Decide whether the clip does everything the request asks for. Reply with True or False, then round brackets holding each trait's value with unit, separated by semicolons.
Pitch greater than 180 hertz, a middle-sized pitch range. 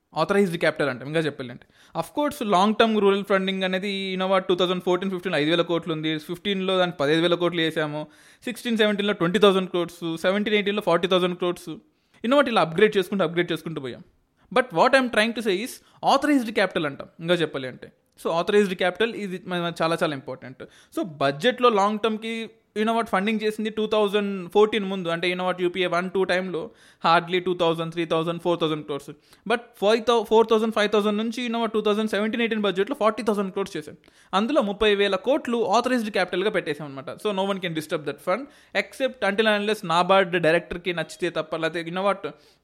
True (190 Hz; 4.2 semitones)